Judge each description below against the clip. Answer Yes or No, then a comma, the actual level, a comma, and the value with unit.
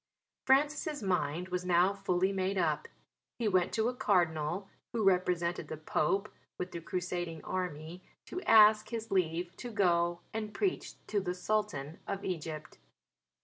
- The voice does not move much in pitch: No, average, 3.6 semitones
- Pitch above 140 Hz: Yes, medium, 185 Hz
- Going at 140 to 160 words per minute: Yes, average, 145 wpm